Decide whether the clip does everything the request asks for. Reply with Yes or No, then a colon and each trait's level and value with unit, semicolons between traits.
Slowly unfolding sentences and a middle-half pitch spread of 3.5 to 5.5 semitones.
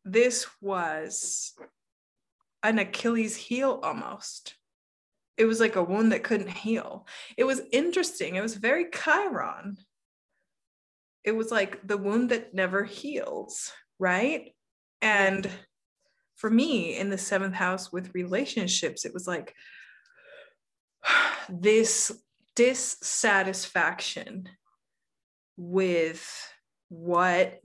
Yes: slow, 100 wpm; average, 3.9 semitones